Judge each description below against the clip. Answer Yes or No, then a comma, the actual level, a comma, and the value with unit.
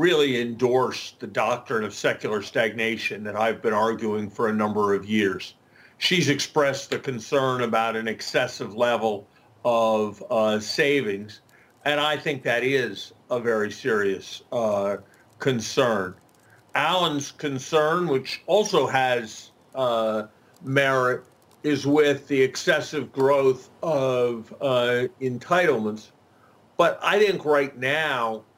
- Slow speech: Yes, slow, 120 wpm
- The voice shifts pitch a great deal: No, average, 4.3 semitones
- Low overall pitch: Yes, low, 125 Hz